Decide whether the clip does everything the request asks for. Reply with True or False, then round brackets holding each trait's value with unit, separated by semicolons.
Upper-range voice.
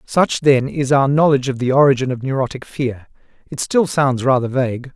False (135 Hz)